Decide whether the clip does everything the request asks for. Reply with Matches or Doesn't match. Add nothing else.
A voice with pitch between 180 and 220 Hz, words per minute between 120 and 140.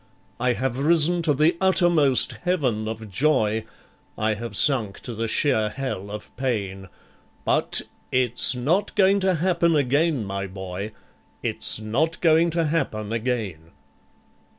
Doesn't match